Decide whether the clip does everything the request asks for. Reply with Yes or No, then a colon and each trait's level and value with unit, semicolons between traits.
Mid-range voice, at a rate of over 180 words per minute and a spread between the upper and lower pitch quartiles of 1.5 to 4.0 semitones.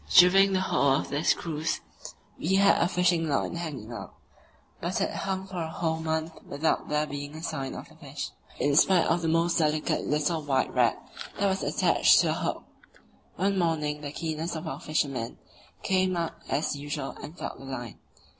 Yes: medium, 160 Hz; average, 190 wpm; average, 3.1 semitones